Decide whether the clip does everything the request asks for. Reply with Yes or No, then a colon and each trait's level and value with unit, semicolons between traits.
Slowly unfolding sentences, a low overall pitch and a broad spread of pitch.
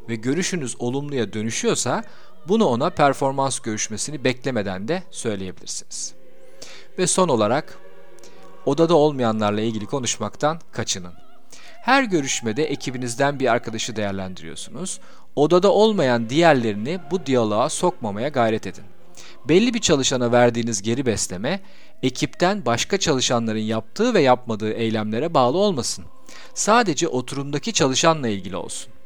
No: average, 110 wpm; low, 130 Hz; wide, 6.9 semitones